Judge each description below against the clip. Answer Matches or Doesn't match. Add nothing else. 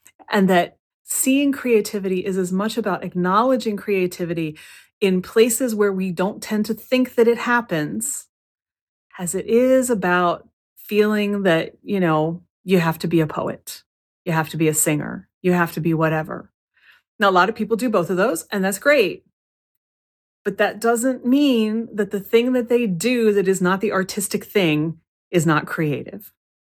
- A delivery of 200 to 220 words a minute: Doesn't match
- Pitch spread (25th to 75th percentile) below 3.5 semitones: Doesn't match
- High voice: Matches